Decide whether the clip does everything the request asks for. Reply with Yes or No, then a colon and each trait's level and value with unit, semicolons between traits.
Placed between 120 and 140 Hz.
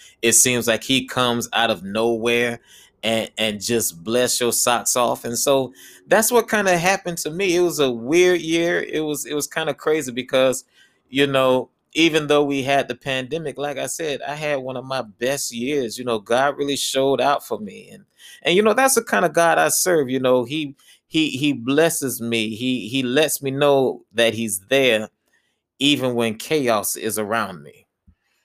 Yes: low, 135 Hz